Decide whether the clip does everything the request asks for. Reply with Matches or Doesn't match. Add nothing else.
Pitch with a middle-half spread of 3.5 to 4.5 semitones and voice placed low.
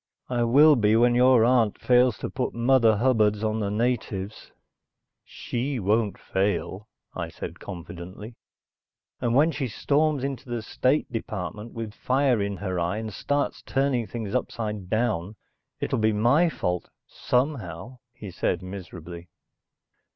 Matches